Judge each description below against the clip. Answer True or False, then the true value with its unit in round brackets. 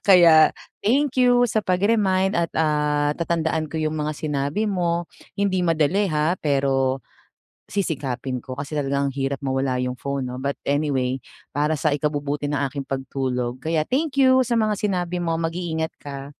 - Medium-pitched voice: True (155 Hz)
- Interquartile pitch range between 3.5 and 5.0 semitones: True (4.5 semitones)